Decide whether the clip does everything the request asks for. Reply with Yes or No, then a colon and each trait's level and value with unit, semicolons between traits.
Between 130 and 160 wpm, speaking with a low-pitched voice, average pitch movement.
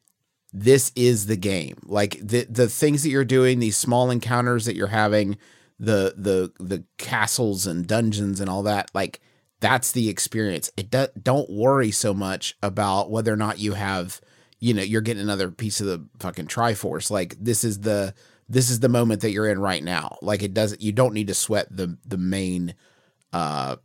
No: average, 195 wpm; low, 105 Hz; average, 3.6 semitones